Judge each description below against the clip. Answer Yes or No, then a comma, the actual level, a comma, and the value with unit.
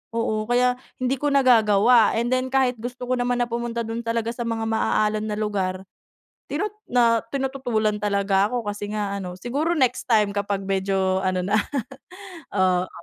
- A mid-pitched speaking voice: No, high, 225 Hz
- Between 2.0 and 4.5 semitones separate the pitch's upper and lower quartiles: Yes, average, 3.5 semitones